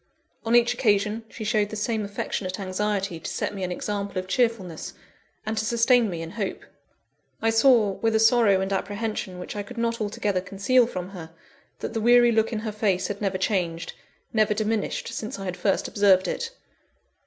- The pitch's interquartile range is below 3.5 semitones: Yes, average, 2.8 semitones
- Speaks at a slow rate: No, average, 190 wpm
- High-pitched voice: Yes, high, 210 Hz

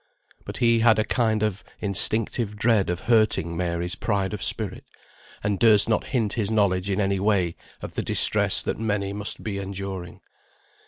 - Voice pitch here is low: Yes, low, 100 Hz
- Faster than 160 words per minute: Yes, average, 170 wpm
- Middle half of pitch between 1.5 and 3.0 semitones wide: Yes, narrow, 2.4 semitones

